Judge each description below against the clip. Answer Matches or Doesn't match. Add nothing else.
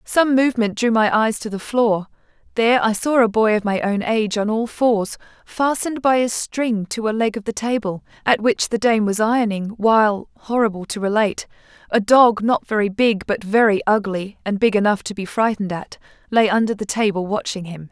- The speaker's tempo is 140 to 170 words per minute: Doesn't match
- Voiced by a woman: Matches